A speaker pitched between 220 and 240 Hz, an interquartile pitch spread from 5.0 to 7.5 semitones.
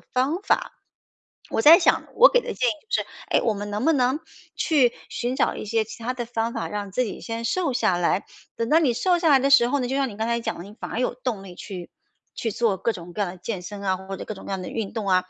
No: high, 230 Hz; average, 4.5 semitones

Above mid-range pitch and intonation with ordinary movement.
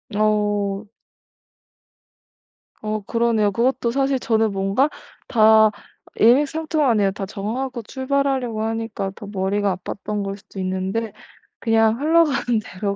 Yes: high, 220 Hz; average, 3.6 semitones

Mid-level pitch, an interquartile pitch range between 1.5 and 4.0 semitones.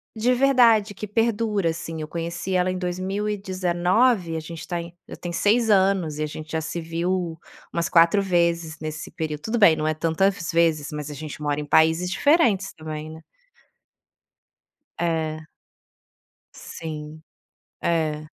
Yes: medium, 170 Hz; average, 3.7 semitones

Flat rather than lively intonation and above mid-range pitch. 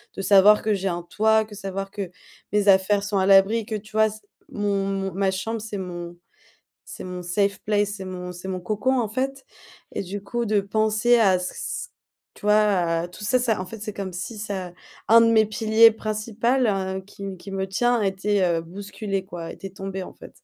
Yes: narrow, 2.2 semitones; high, 200 Hz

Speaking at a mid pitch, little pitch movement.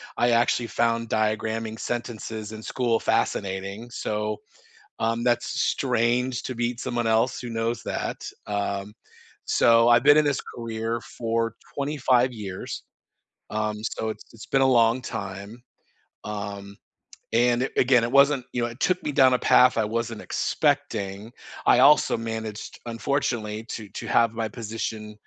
No: low, 115 Hz; narrow, 2.1 semitones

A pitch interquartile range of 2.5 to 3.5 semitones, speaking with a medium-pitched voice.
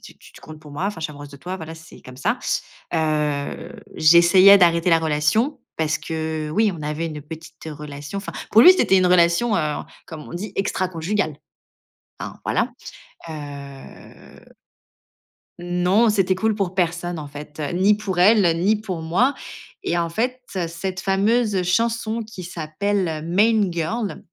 No: average, 4.3 semitones; medium, 175 Hz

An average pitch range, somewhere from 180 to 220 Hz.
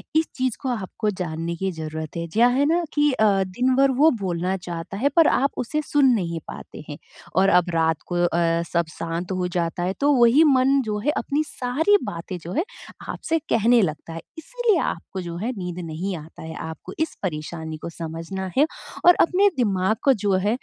No: wide, 8.0 semitones; high, 190 Hz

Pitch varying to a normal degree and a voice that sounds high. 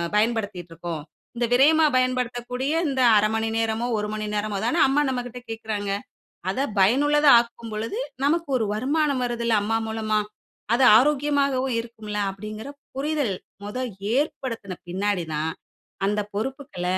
Yes: average, 4.1 semitones; high, 235 Hz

